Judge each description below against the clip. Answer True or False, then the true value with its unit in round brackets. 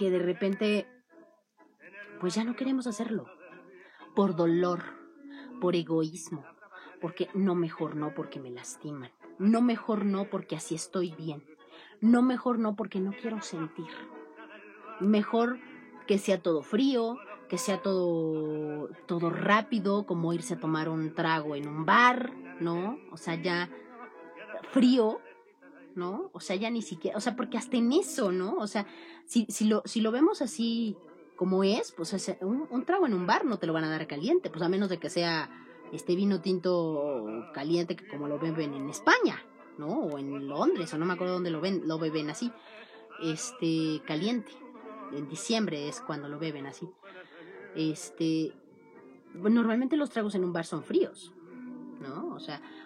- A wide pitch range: True (5.9 semitones)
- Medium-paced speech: True (170 wpm)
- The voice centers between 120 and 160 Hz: False (185 Hz)